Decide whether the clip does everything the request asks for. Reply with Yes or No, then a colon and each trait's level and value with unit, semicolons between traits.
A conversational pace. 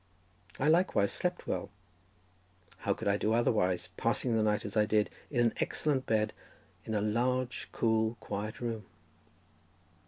Yes: average, 150 wpm